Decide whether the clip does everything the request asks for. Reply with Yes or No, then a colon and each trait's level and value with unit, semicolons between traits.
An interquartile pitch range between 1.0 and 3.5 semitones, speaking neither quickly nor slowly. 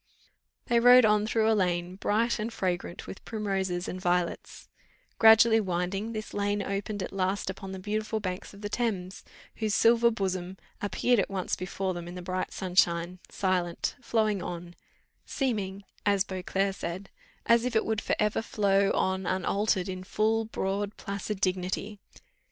Yes: average, 2.8 semitones; average, 160 wpm